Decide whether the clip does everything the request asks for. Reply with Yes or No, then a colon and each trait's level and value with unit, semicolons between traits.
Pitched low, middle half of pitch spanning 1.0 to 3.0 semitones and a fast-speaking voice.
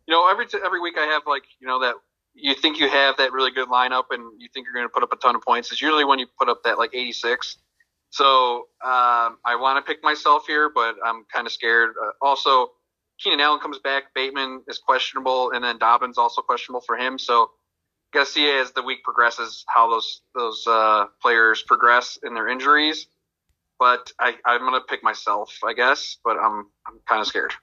No: low, 130 Hz; average, 3.8 semitones; fast, 215 wpm